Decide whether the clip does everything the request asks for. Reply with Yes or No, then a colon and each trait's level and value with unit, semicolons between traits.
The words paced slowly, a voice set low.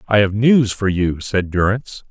No: average, 200 wpm; low, 105 Hz